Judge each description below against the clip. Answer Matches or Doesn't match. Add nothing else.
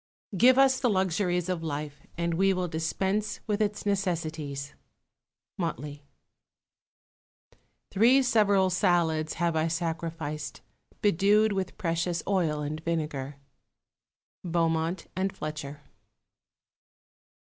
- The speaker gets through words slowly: Matches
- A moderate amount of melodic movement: Matches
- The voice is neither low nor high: Matches